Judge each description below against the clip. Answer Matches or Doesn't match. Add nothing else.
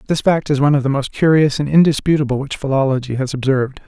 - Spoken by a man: Matches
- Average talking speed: Doesn't match